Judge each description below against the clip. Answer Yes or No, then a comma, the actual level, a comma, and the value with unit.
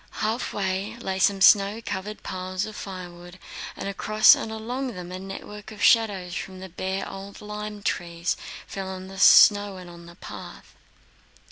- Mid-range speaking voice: No, high, 195 Hz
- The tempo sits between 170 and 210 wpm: No, average, 160 wpm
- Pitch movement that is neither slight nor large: No, narrow, 2.2 semitones